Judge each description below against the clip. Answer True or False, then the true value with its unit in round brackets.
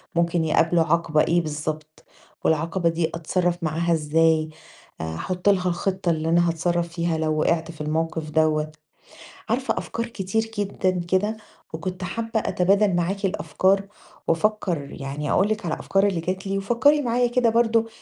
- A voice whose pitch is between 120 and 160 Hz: False (170 Hz)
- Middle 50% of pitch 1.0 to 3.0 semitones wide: False (3.5 semitones)